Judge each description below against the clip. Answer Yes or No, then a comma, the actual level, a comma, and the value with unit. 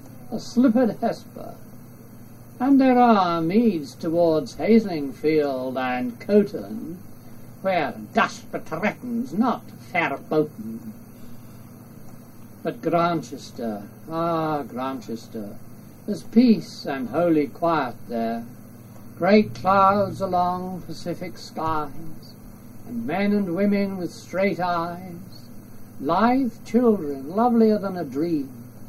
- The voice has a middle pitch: Yes, medium, 155 Hz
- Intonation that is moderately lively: No, wide, 8.7 semitones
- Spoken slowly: Yes, slow, 95 wpm